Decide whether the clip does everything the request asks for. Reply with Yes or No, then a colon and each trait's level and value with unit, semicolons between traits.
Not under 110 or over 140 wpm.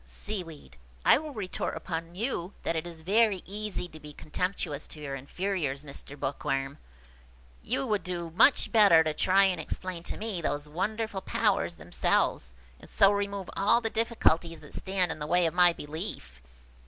No: average, 170 wpm